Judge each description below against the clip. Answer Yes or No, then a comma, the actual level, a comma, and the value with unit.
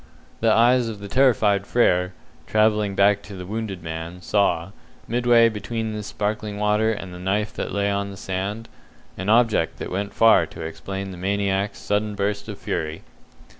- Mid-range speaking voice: No, low, 100 Hz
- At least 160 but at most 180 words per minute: Yes, average, 170 wpm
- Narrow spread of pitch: Yes, narrow, 2.1 semitones